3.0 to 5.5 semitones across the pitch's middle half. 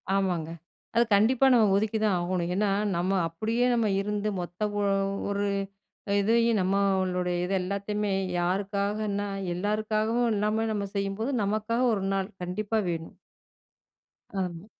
No: narrow, 2.4 semitones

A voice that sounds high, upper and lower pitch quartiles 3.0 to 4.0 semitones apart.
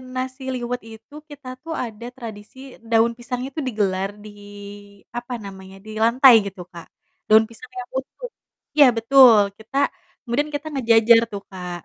Yes: high, 235 Hz; average, 3.6 semitones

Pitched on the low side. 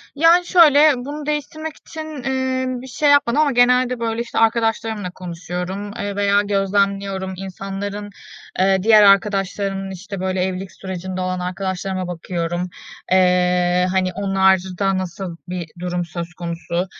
No: high, 195 Hz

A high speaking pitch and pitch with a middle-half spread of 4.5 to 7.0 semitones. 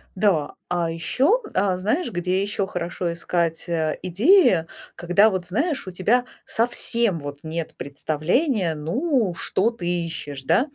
No: medium, 180 Hz; average, 5.3 semitones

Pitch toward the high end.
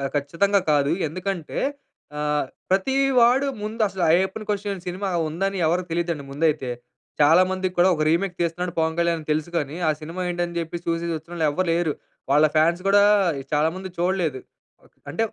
No: medium, 170 Hz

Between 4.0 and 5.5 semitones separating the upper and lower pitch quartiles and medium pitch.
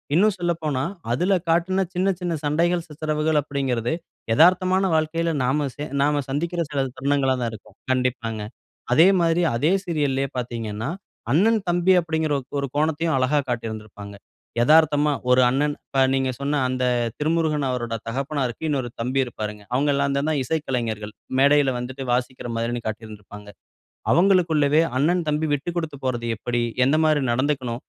Yes: average, 4.4 semitones; medium, 145 Hz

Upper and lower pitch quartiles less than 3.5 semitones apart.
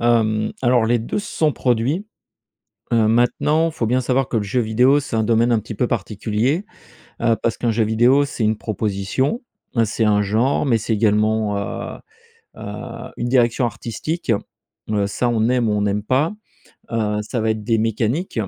Yes: average, 2.7 semitones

